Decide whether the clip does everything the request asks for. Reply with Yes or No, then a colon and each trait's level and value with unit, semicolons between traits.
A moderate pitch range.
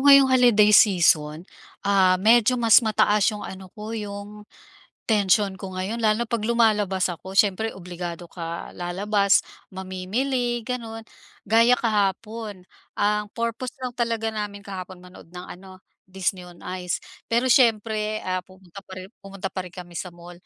Yes: average, 3.3 semitones